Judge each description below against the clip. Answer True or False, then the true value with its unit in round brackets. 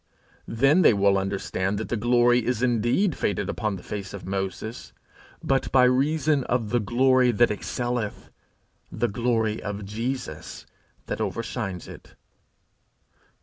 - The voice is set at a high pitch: False (115 Hz)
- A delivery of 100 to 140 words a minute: True (135 wpm)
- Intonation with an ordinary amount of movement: True (3.7 semitones)